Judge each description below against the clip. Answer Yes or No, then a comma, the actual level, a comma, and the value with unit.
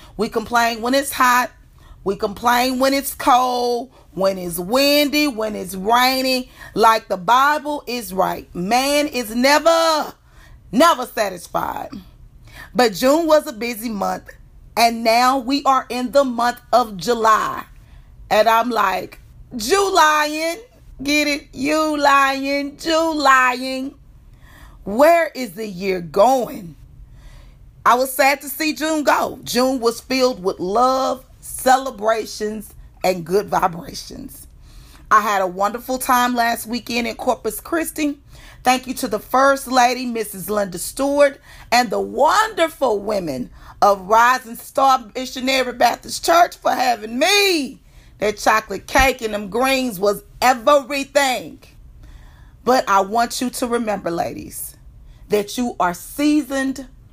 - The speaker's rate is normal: No, slow, 130 wpm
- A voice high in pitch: Yes, very high, 250 Hz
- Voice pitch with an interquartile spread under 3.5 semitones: No, average, 4.3 semitones